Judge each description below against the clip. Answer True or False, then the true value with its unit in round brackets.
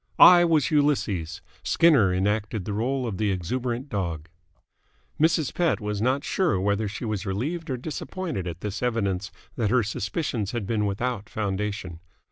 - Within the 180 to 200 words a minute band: False (155 wpm)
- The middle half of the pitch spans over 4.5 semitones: True (5.1 semitones)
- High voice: False (110 Hz)